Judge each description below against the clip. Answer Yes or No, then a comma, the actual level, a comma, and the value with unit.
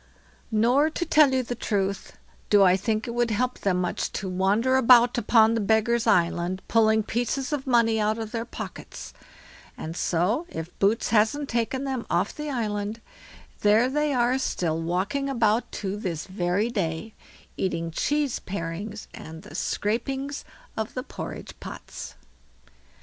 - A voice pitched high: Yes, high, 220 Hz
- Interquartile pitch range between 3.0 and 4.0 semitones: No, average, 4.5 semitones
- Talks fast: No, average, 155 wpm